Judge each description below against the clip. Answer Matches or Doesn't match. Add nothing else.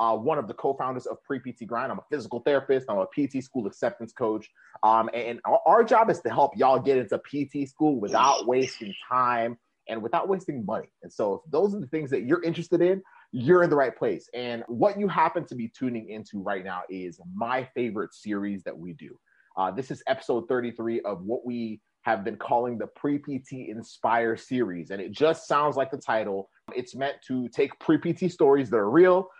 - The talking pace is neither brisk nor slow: Doesn't match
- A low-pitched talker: Matches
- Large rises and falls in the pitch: Doesn't match